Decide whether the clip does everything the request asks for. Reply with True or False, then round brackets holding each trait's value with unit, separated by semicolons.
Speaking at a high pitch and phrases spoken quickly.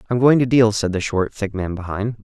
False (110 Hz; 265 wpm)